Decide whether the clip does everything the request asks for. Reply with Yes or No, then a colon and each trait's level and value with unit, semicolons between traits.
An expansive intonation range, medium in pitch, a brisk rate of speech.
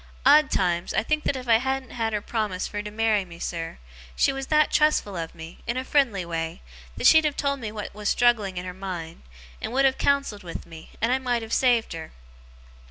No: wide, 6.4 semitones; high, 220 Hz; fast, 230 wpm